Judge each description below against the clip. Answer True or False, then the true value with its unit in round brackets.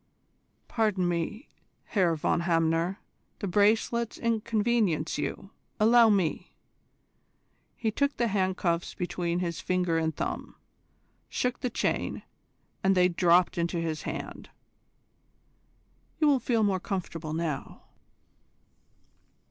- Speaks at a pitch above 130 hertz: True (185 Hz)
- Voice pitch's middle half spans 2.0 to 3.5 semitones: False (4.6 semitones)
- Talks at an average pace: False (110 wpm)